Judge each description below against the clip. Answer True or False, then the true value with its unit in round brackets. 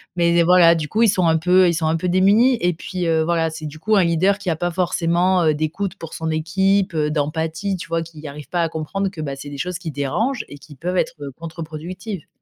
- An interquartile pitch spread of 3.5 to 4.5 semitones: False (2.7 semitones)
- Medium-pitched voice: True (170 Hz)